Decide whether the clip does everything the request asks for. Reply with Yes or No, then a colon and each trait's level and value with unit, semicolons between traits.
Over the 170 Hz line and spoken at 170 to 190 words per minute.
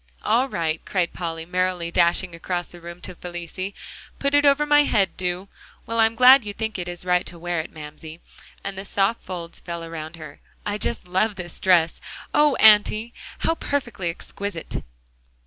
Yes: medium, 185 Hz; average, 180 wpm